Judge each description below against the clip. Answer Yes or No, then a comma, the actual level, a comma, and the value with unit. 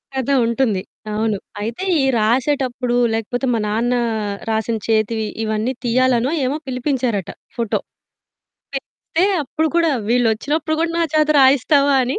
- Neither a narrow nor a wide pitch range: Yes, average, 3.6 semitones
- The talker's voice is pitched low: No, very high, 250 Hz